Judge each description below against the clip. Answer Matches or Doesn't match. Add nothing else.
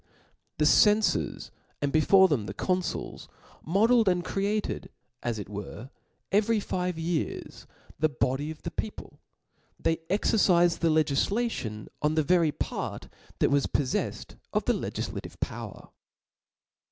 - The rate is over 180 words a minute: Doesn't match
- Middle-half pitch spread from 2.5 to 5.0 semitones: Doesn't match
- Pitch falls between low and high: Matches